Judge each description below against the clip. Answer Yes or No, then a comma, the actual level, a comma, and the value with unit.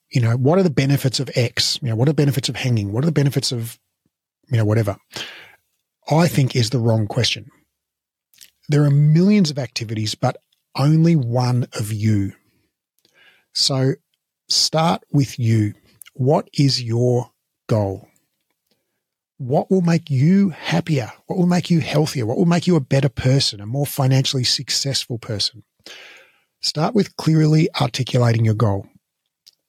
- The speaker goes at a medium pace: Yes, average, 155 wpm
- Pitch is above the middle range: No, low, 135 Hz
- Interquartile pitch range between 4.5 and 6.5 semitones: Yes, average, 4.8 semitones